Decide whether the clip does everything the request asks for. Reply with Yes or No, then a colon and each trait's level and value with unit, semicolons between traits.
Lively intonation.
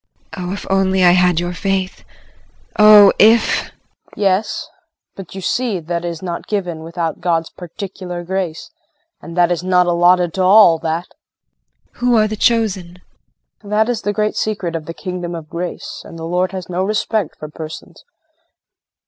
No: average, 2.7 semitones